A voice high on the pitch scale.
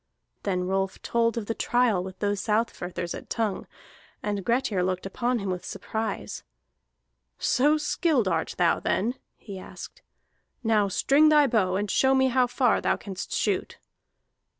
Yes: high, 215 Hz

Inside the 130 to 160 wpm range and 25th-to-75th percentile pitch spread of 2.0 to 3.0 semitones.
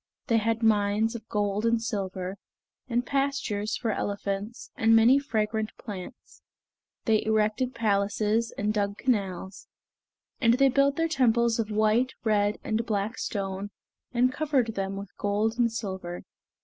Yes: average, 140 wpm; narrow, 2.6 semitones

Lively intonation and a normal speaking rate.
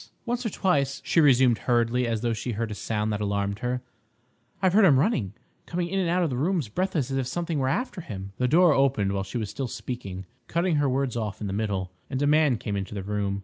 No: wide, 7.1 semitones; fast, 240 wpm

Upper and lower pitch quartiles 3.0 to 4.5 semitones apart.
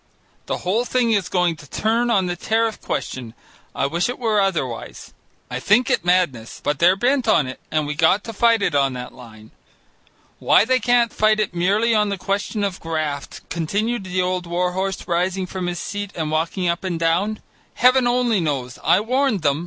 No: average, 4.9 semitones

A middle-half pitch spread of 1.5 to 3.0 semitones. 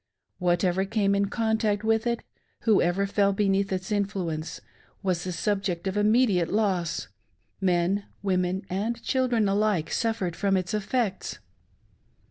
Yes: average, 2.7 semitones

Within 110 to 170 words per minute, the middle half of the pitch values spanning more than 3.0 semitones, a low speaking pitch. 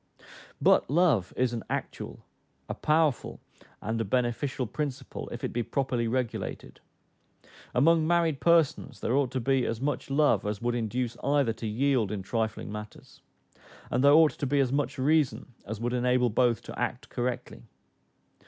Yes: average, 160 wpm; average, 3.7 semitones; low, 125 Hz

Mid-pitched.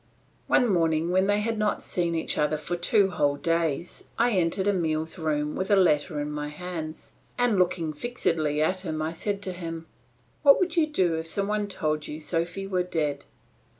Yes: medium, 170 Hz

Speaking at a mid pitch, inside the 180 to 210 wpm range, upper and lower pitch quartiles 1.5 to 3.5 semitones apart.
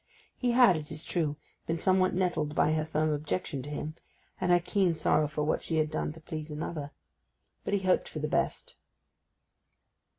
Yes: medium, 155 Hz; average, 190 wpm; average, 3.0 semitones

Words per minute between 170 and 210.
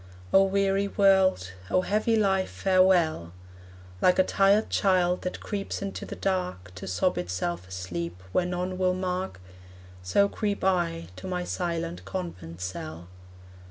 No: average, 140 wpm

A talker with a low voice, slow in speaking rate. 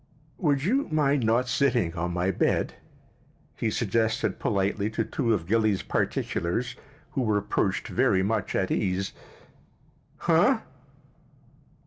Yes: low, 110 Hz; slow, 120 wpm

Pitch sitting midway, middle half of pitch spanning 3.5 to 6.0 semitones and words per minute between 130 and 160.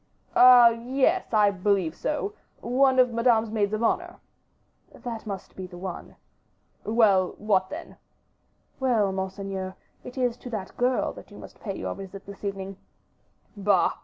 No: high, 215 Hz; average, 4.1 semitones; average, 155 wpm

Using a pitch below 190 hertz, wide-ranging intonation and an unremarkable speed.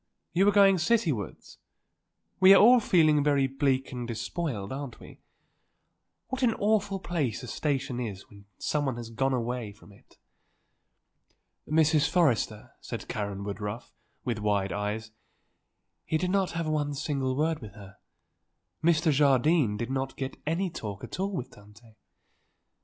Yes: low, 135 Hz; wide, 6.6 semitones; average, 145 wpm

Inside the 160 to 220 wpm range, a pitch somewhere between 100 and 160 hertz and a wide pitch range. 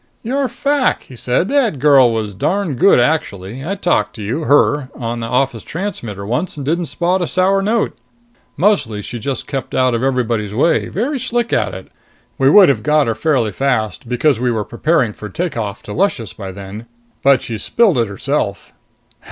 Yes: average, 185 wpm; low, 135 Hz; wide, 7.8 semitones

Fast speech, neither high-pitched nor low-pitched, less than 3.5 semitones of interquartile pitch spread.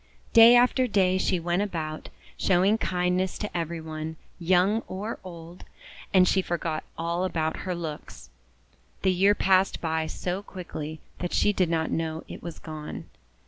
No: average, 160 wpm; medium, 175 Hz; average, 2.8 semitones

